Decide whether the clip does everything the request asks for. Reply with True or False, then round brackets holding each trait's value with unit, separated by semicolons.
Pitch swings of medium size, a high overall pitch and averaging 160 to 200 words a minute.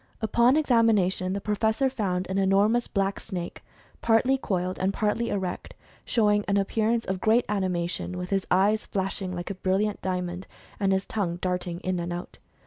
True (3.0 semitones; 195 Hz; 170 wpm)